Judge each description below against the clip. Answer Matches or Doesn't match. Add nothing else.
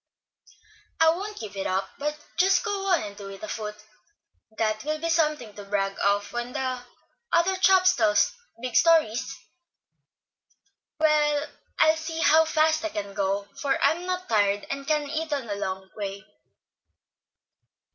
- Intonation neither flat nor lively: Doesn't match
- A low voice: Doesn't match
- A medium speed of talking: Matches